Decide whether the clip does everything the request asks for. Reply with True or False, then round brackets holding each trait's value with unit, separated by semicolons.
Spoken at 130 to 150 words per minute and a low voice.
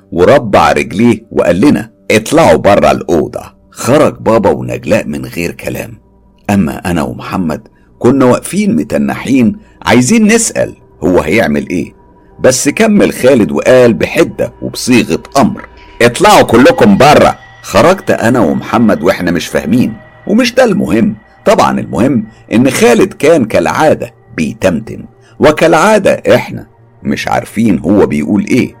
False (115 wpm; 130 Hz)